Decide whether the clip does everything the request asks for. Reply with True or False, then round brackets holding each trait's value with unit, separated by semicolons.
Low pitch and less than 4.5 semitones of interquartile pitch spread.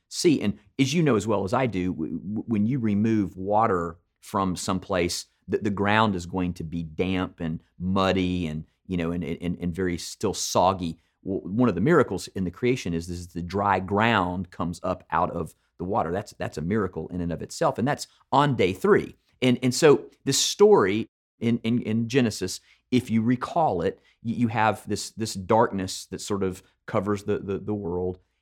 True (95 Hz; 3.8 semitones)